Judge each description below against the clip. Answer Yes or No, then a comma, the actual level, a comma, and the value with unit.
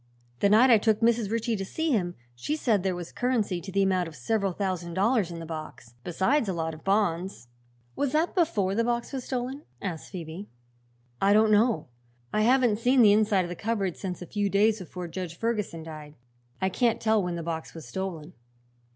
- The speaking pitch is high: Yes, high, 200 Hz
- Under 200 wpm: No, fast, 205 wpm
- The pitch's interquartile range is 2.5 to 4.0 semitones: No, average, 4.7 semitones